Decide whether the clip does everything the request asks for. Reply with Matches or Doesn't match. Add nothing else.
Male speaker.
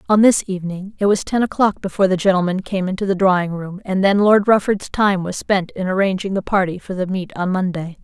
Doesn't match